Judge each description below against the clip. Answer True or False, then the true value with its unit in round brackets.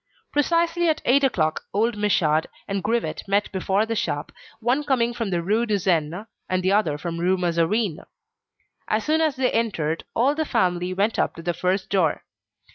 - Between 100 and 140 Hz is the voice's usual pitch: False (200 Hz)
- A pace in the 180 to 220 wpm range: True (190 wpm)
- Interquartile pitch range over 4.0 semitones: True (5.2 semitones)